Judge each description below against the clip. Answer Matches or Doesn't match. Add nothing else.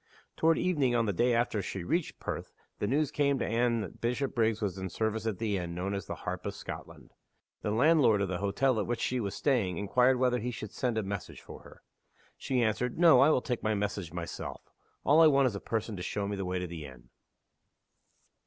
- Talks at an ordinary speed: Doesn't match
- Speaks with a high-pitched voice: Doesn't match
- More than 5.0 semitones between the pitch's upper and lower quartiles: Doesn't match